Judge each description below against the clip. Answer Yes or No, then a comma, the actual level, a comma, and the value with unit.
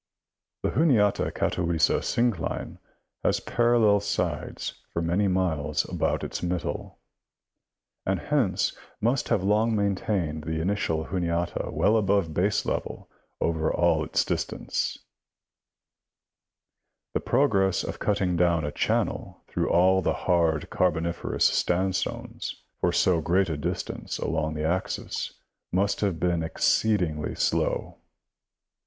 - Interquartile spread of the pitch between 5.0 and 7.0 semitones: No, average, 3.6 semitones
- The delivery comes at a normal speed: No, slow, 115 wpm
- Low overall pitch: Yes, very low, 90 Hz